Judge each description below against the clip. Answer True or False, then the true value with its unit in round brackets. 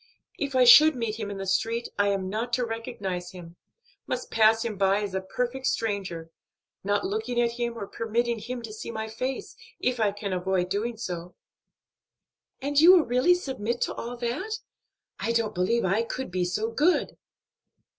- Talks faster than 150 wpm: True (185 wpm)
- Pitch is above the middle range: True (225 Hz)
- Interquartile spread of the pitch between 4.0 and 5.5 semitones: False (3.6 semitones)